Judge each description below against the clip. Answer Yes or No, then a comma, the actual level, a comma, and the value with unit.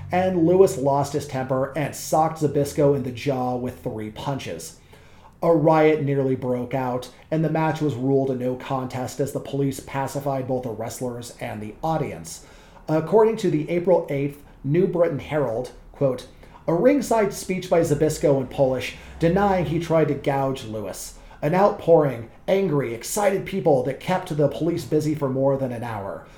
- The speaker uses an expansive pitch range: No, average, 4.0 semitones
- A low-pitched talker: No, medium, 145 Hz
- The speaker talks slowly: No, average, 170 wpm